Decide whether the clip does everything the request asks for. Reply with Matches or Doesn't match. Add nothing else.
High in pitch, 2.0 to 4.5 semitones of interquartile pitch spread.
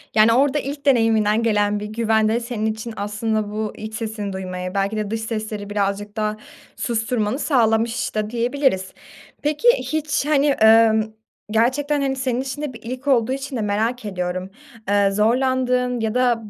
Matches